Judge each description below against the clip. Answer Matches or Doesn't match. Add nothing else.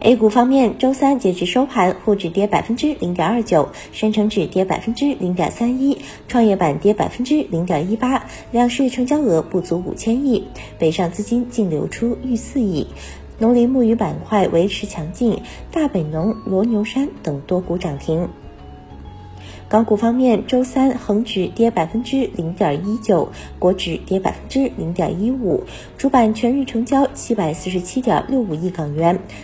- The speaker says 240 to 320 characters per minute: Matches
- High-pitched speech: Matches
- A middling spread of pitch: Doesn't match